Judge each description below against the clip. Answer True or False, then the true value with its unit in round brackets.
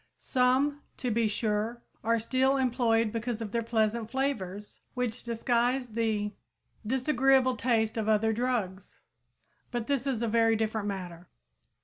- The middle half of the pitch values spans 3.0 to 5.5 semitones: False (2.6 semitones)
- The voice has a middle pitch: False (230 Hz)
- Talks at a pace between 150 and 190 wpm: False (135 wpm)